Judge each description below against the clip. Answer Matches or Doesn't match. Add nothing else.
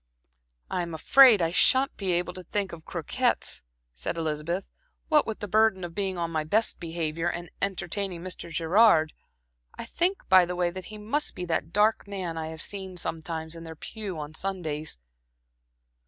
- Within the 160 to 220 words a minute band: Matches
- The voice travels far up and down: Doesn't match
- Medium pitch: Matches